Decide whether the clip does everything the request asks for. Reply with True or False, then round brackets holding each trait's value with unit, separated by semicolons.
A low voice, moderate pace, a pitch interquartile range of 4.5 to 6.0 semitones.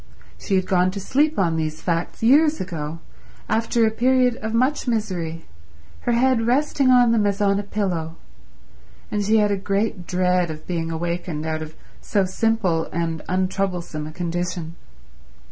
False (190 Hz; 160 wpm; 5.1 semitones)